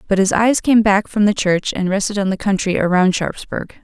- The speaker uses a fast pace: Yes, fast, 235 wpm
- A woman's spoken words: Yes, female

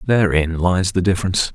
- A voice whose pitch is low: Yes, very low, 90 Hz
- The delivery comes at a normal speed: Yes, average, 155 wpm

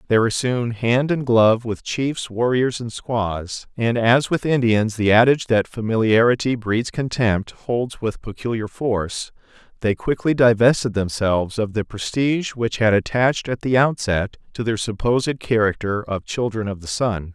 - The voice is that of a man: Yes, male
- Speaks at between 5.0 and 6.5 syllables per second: No, 4.6 syllables/s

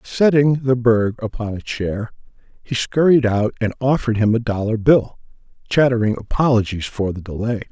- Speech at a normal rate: Yes, average, 155 wpm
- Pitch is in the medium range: No, low, 115 Hz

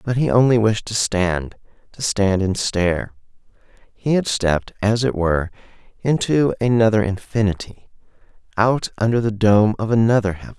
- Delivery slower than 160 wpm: Yes, average, 145 wpm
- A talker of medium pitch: No, low, 105 Hz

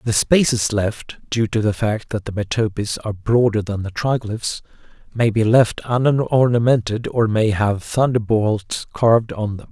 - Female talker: No, male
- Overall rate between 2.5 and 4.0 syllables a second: Yes, 2.8 syllables/s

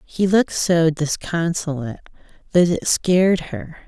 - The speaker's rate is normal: No, slow, 125 wpm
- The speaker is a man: No, female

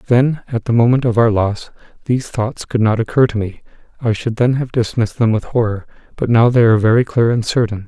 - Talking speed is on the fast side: Yes, fast, 230 wpm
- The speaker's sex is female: No, male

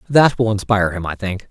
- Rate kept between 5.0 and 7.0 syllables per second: Yes, 6.0 syllables/s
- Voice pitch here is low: Yes, low, 105 Hz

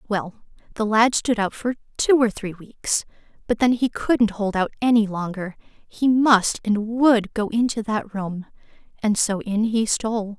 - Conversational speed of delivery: Yes, average, 180 wpm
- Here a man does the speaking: No, female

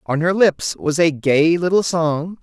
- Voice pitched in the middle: Yes, medium, 165 Hz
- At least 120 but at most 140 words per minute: No, average, 200 wpm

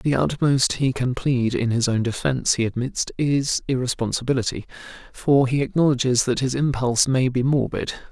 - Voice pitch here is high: No, low, 130 Hz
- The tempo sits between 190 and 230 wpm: No, average, 165 wpm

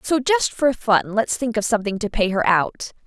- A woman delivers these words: Yes, female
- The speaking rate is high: Yes, fast, 235 wpm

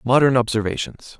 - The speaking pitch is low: Yes, low, 125 Hz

